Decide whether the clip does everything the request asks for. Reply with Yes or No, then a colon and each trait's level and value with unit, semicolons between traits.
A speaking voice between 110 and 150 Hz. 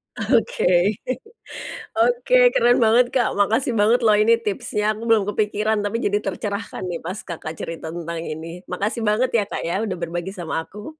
No: high, 210 Hz